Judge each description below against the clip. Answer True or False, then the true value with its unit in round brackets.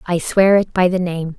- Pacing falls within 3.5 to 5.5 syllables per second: True (4.7 syllables/s)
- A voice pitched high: False (180 Hz)